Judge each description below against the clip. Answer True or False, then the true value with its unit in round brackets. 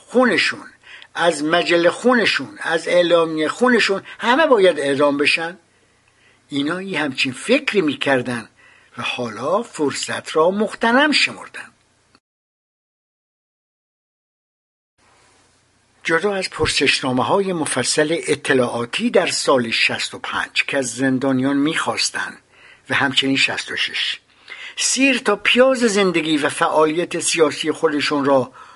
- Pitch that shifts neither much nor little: False (6.2 semitones)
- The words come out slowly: True (100 wpm)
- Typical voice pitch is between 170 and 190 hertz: False (160 Hz)